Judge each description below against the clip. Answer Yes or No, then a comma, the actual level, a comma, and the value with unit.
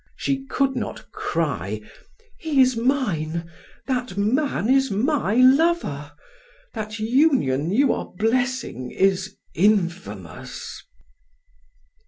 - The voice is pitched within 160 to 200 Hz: No, high, 225 Hz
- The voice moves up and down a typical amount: No, wide, 6.8 semitones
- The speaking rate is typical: No, slow, 95 wpm